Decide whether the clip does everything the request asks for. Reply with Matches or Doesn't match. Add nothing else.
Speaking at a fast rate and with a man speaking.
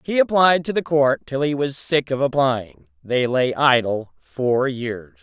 Doesn't match